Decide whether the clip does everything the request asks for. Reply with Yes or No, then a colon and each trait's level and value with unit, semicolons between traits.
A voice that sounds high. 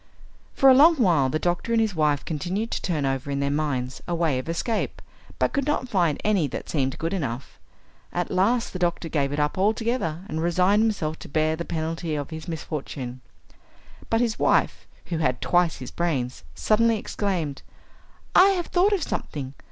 No: medium, 165 Hz